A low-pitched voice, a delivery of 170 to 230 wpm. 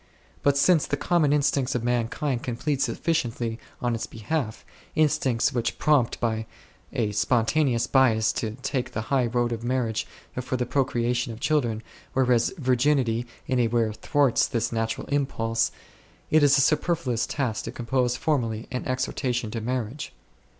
No: low, 125 Hz; average, 155 wpm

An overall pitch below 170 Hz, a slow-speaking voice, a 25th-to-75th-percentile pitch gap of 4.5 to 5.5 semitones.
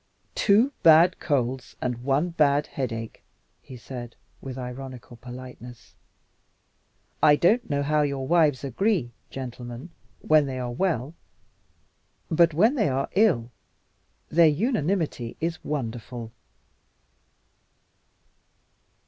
Yes: medium, 140 Hz; slow, 105 wpm; average, 5.1 semitones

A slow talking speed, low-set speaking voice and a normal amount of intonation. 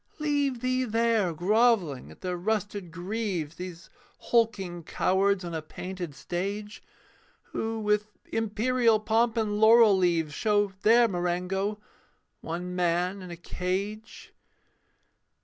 No: slow, 115 wpm; high, 200 Hz; average, 3.9 semitones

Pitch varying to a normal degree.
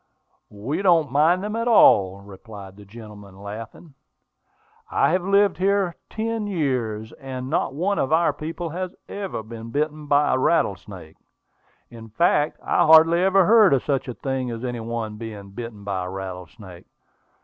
No: wide, 8.3 semitones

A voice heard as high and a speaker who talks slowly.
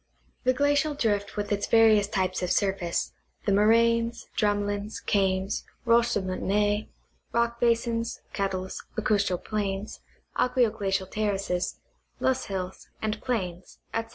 Yes: high, 205 Hz; slow, 130 wpm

